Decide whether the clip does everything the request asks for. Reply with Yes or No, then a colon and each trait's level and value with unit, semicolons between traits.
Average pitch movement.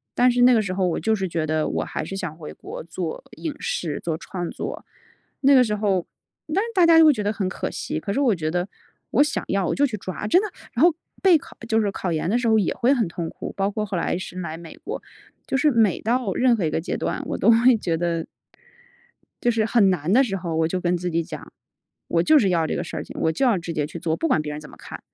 No: wide, 6.1 semitones